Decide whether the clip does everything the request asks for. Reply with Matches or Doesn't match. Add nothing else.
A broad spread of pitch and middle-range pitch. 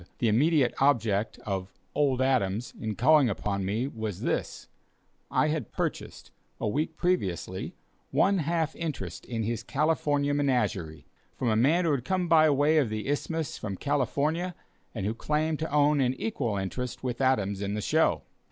Doesn't match